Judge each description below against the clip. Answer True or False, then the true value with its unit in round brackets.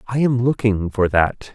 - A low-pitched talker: True (110 Hz)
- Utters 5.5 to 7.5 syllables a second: False (4.3 syllables/s)